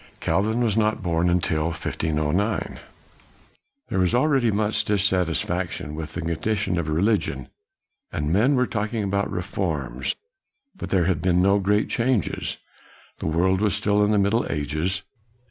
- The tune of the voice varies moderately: Yes, average, 4.4 semitones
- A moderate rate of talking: Yes, average, 145 wpm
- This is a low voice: Yes, very low, 95 Hz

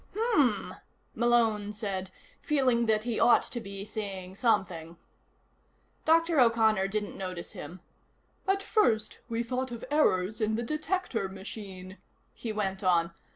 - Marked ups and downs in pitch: No, average, 3.9 semitones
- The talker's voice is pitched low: No, high, 215 Hz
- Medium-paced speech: No, slow, 130 wpm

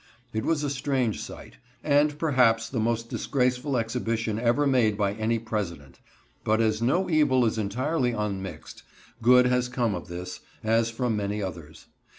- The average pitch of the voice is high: No, low, 115 Hz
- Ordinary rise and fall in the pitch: Yes, average, 3.0 semitones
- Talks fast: No, average, 160 wpm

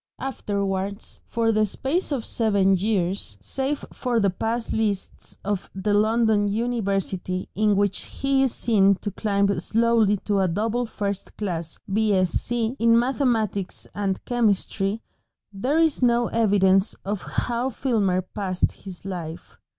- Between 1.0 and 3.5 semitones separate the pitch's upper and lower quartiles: Yes, average, 3.2 semitones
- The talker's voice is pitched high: Yes, high, 210 Hz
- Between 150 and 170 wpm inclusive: No, slow, 135 wpm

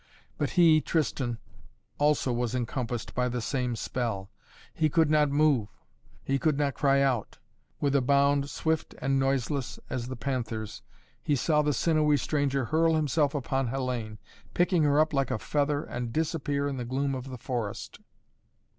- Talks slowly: No, average, 165 wpm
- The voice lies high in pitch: No, low, 135 Hz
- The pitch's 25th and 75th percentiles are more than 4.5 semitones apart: No, average, 3.2 semitones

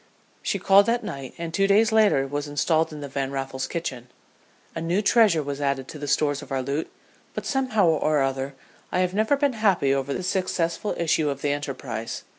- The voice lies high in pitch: No, medium, 155 Hz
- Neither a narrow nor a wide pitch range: No, wide, 5.9 semitones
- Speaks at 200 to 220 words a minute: Yes, fast, 205 wpm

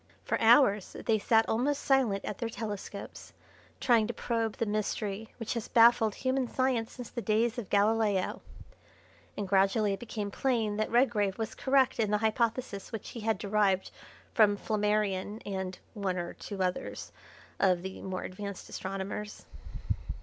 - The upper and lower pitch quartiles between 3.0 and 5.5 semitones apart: No, narrow, 2.6 semitones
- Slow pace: No, average, 155 wpm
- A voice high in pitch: Yes, high, 215 Hz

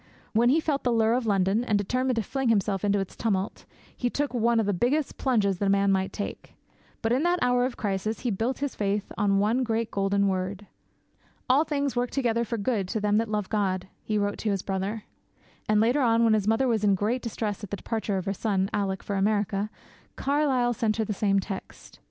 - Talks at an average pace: No, fast, 225 wpm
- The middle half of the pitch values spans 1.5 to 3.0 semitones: No, average, 3.4 semitones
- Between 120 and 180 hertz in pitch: No, high, 215 Hz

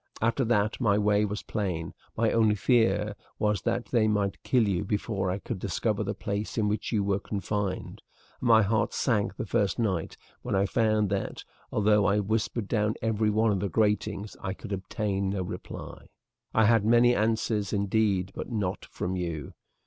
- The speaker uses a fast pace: No, average, 180 wpm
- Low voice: Yes, low, 105 Hz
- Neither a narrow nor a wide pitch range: No, narrow, 2.0 semitones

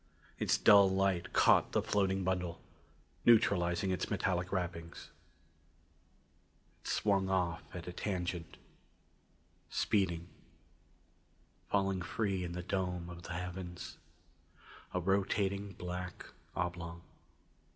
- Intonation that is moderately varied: No, narrow, 1.8 semitones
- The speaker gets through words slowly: Yes, slow, 100 wpm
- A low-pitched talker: Yes, very low, 90 Hz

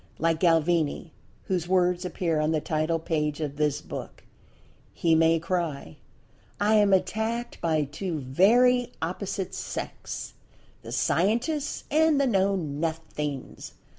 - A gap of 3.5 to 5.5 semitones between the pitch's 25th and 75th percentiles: Yes, average, 4.2 semitones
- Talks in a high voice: No, medium, 170 Hz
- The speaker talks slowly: Yes, slow, 120 wpm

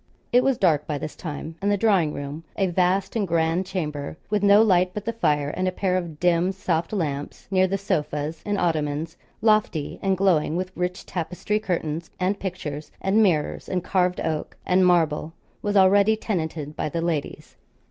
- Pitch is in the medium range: Yes, medium, 180 Hz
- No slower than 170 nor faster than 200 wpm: Yes, average, 185 wpm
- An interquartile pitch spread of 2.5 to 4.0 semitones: Yes, average, 3.6 semitones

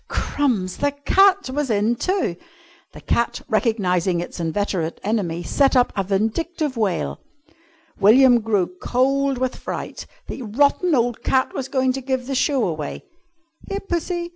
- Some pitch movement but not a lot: No, wide, 5.8 semitones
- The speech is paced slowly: No, average, 145 wpm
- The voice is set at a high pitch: Yes, high, 245 Hz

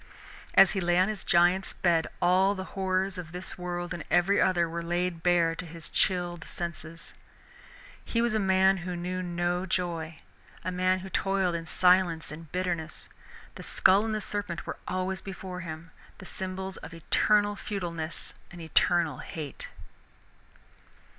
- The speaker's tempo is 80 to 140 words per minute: No, average, 160 wpm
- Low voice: No, medium, 180 Hz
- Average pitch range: No, narrow, 1.9 semitones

